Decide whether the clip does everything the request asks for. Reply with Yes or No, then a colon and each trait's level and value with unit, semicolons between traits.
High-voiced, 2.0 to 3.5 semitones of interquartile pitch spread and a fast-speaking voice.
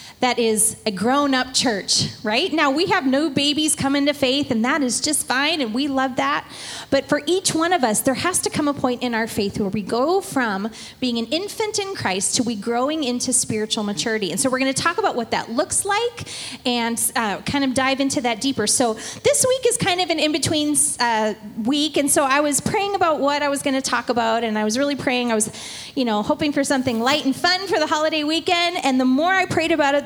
No: very high, 275 Hz; average, 4.4 semitones; fast, 240 wpm